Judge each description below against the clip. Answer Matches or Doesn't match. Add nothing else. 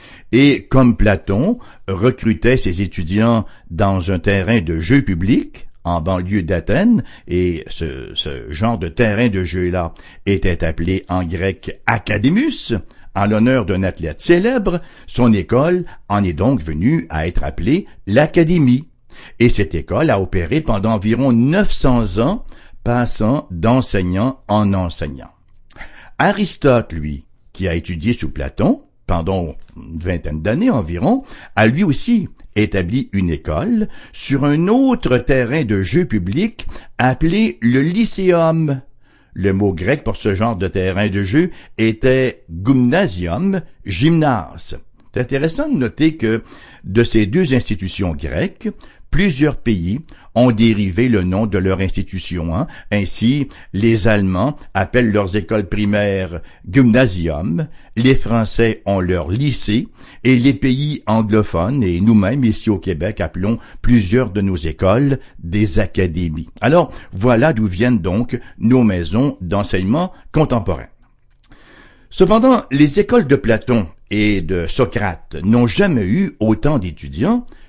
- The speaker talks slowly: Matches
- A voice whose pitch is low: Matches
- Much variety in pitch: Matches